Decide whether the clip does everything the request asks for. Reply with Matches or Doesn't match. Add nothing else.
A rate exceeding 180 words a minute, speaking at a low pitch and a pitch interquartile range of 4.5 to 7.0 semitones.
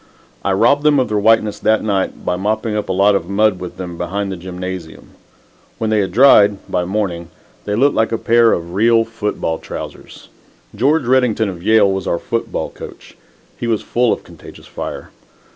Doesn't match